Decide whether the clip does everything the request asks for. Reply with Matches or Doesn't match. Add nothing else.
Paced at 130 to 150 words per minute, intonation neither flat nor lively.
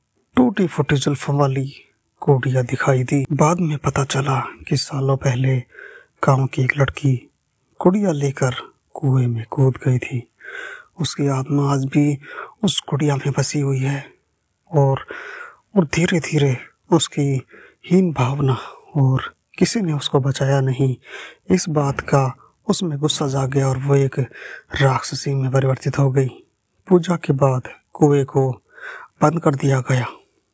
Doesn't match